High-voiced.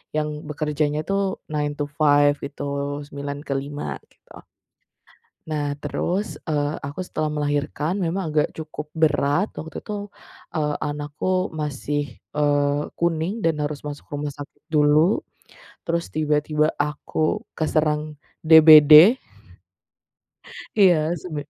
No: medium, 150 Hz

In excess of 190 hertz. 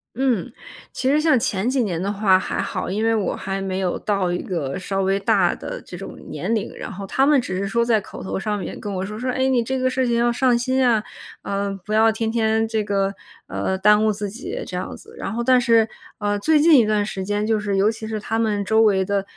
Yes: high, 215 Hz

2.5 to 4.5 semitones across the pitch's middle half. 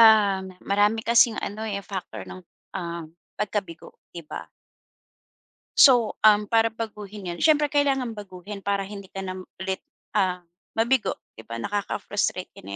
Yes: average, 3.0 semitones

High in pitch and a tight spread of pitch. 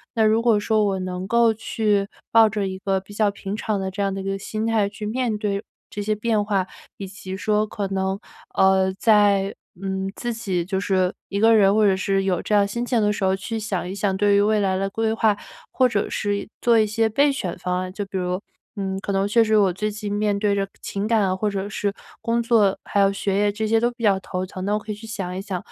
Yes: high, 205 Hz; narrow, 2.0 semitones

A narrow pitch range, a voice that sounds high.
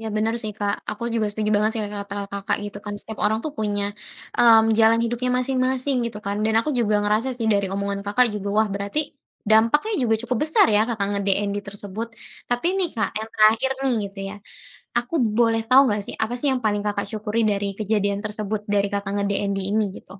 Yes: narrow, 2.3 semitones; high, 215 Hz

